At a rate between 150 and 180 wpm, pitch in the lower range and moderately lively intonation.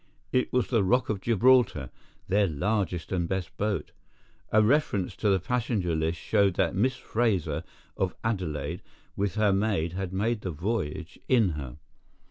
Yes: average, 155 wpm; low, 100 Hz; average, 4.1 semitones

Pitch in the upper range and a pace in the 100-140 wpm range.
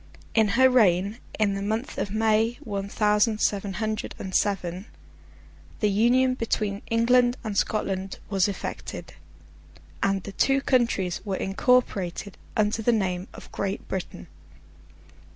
Yes: high, 210 Hz; slow, 135 wpm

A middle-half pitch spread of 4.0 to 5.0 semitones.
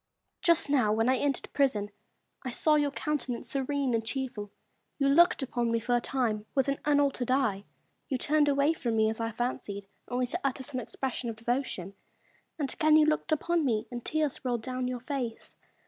No: average, 3.6 semitones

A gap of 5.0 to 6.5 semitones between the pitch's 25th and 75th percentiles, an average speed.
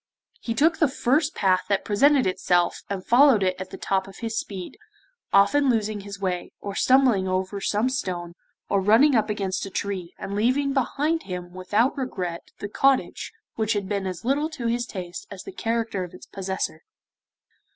Yes: average, 5.3 semitones; average, 180 wpm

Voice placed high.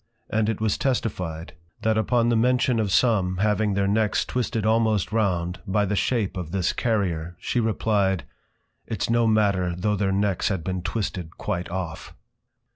No: low, 105 Hz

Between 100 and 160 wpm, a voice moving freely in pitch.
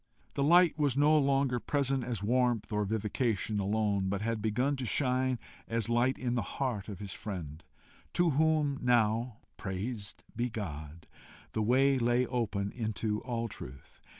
No: average, 155 wpm; average, 3.9 semitones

